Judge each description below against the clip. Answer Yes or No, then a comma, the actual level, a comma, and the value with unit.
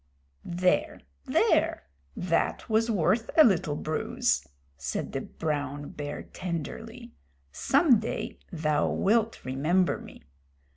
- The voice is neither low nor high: Yes, medium, 175 Hz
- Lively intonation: Yes, wide, 7.2 semitones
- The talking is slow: Yes, slow, 105 wpm